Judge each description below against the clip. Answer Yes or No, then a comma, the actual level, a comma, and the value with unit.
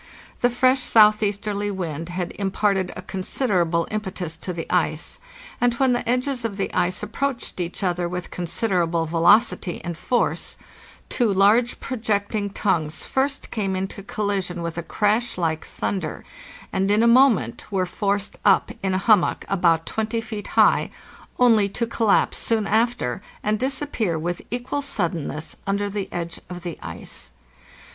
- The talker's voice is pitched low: No, high, 200 Hz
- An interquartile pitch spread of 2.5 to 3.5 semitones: No, average, 4.3 semitones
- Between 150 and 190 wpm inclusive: Yes, average, 155 wpm